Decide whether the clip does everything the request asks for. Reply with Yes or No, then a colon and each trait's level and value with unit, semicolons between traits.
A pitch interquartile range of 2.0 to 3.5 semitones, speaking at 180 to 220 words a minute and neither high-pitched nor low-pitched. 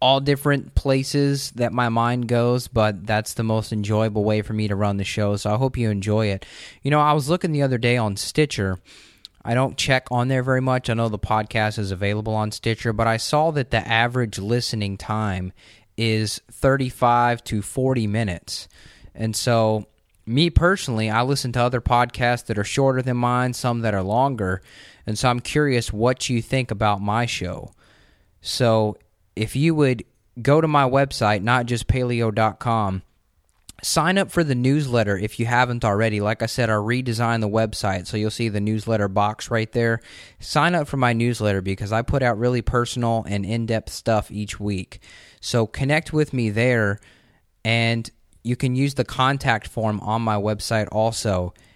No: average, 3.0 semitones; average, 185 wpm; low, 115 Hz